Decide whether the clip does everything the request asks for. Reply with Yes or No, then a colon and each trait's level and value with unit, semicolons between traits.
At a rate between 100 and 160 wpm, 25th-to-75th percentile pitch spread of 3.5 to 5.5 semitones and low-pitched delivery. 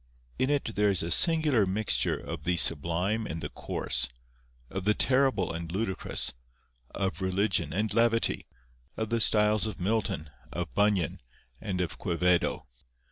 Yes: average, 145 wpm; average, 4.1 semitones; low, 100 Hz